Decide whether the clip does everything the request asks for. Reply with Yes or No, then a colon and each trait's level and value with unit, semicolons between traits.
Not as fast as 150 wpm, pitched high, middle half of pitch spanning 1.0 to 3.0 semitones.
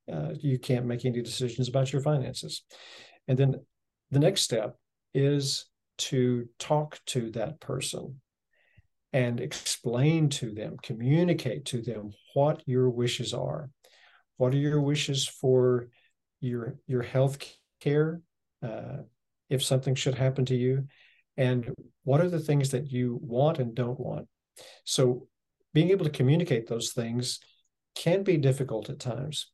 No: average, 140 wpm; low, 130 Hz; narrow, 2.5 semitones